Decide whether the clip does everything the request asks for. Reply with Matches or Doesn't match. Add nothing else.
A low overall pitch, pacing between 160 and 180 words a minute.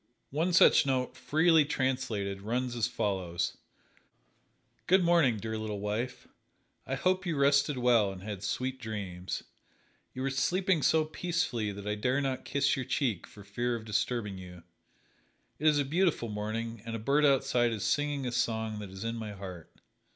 Matches